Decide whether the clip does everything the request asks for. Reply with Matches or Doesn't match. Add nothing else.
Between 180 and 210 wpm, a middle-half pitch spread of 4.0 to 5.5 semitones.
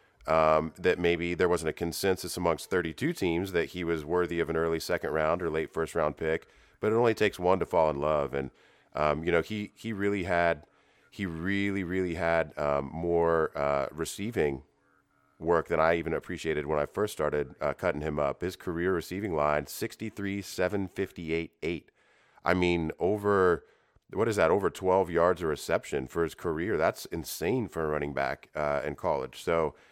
Doesn't match